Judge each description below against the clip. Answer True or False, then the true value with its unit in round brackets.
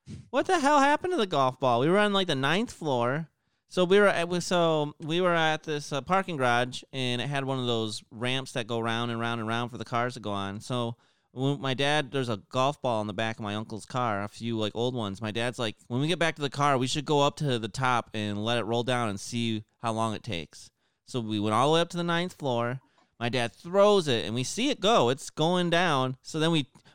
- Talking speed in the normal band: False (270 wpm)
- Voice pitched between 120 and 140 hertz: True (130 Hz)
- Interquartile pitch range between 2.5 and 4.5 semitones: False (5.5 semitones)